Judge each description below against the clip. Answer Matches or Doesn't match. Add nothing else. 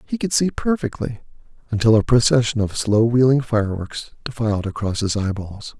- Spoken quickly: Doesn't match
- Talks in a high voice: Doesn't match